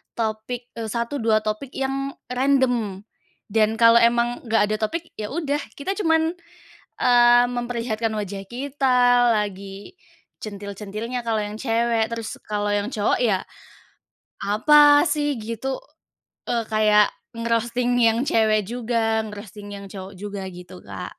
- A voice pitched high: Yes, high, 230 Hz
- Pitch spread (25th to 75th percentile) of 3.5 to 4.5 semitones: No, average, 2.7 semitones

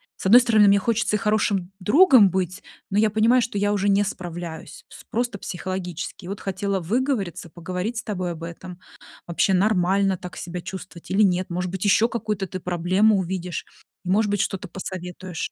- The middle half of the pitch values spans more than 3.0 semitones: No, average, 2.7 semitones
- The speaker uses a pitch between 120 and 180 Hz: No, high, 190 Hz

